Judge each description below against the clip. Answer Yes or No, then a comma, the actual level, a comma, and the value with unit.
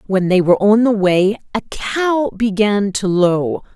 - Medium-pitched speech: No, high, 205 Hz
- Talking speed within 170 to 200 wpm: Yes, average, 175 wpm